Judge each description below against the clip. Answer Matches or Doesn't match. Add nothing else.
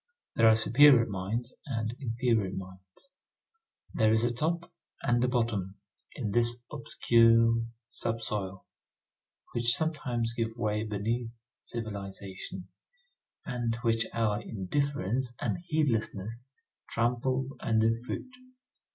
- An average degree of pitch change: Doesn't match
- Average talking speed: Doesn't match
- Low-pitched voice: Matches